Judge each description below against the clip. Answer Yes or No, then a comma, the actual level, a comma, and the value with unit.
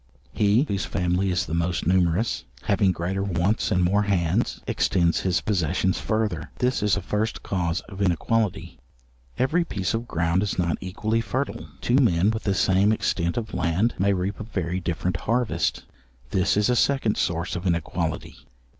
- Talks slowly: No, average, 165 wpm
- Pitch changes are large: No, average, 3.9 semitones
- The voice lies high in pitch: No, very low, 95 Hz